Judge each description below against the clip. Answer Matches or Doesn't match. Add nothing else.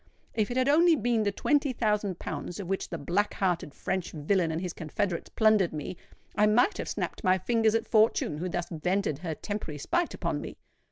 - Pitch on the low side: Doesn't match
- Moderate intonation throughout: Matches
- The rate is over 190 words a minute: Matches